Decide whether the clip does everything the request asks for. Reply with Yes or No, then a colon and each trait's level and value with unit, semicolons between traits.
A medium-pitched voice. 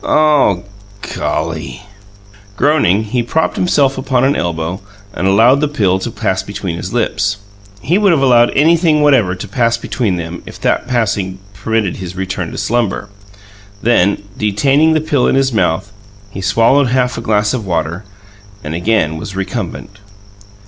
No: low, 105 Hz